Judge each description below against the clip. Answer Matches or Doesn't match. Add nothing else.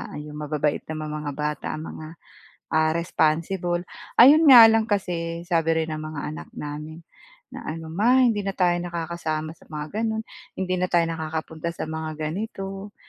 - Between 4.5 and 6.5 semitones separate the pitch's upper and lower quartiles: Doesn't match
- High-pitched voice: Doesn't match